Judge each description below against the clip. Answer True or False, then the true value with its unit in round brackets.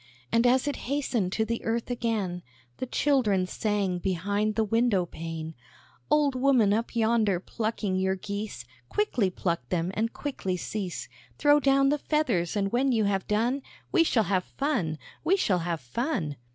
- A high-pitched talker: True (215 Hz)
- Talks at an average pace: True (165 wpm)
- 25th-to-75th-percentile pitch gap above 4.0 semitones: True (5.3 semitones)